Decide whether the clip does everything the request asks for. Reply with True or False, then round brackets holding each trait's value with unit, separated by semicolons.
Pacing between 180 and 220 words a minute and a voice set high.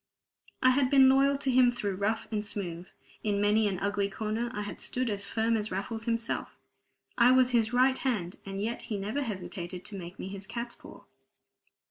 True (190 wpm; 215 Hz)